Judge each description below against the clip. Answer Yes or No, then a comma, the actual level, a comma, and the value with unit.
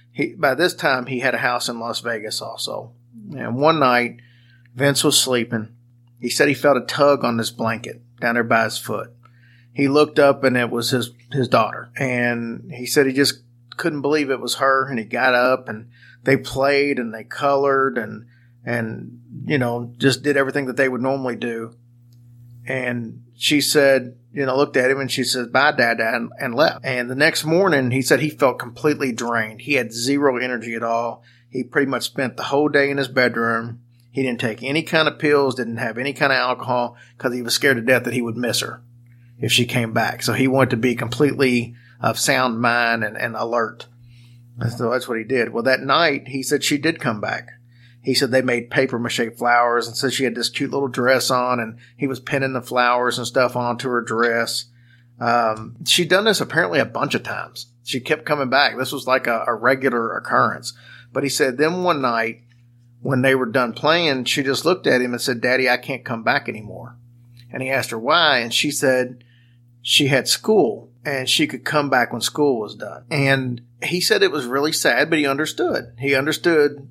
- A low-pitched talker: Yes, low, 125 Hz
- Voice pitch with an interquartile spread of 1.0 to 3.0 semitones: Yes, narrow, 2.4 semitones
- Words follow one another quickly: Yes, fast, 215 wpm